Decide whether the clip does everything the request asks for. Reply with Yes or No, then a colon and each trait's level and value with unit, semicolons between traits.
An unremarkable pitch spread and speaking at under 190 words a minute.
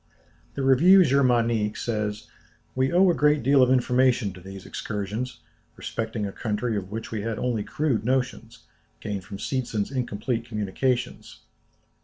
Yes: average, 3.8 semitones; average, 145 wpm